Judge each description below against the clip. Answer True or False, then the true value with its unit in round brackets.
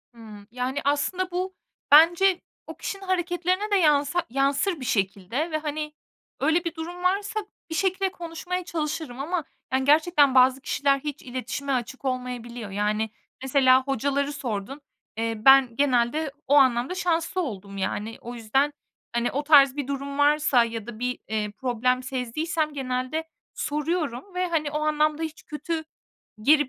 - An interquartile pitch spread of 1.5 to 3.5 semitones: False (4.4 semitones)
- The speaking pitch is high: True (285 Hz)